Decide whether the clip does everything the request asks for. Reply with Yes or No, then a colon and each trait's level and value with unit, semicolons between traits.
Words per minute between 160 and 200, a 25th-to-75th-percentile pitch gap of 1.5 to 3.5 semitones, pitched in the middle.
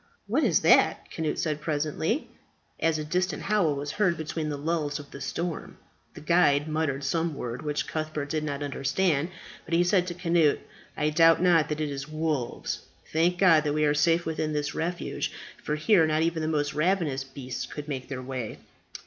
Yes: average, 190 wpm; narrow, 2.4 semitones; medium, 155 Hz